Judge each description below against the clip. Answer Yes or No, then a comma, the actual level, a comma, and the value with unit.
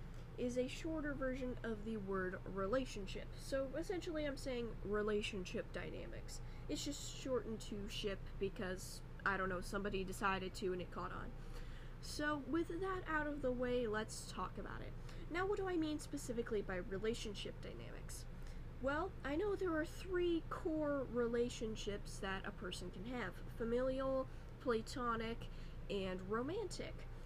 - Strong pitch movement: Yes, wide, 7.2 semitones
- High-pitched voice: Yes, high, 240 Hz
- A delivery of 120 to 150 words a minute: Yes, average, 145 wpm